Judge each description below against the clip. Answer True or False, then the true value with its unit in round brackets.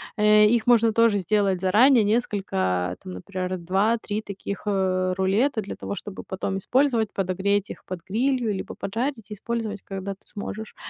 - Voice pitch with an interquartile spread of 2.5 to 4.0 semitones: True (2.9 semitones)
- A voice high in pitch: True (205 Hz)